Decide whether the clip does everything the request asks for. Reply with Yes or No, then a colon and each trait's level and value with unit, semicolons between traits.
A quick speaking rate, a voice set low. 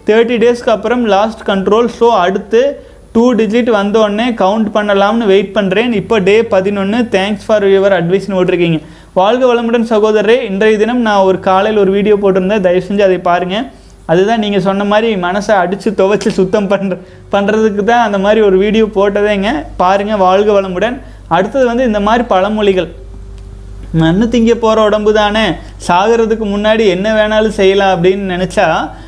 No: fast, 150 wpm; high, 210 Hz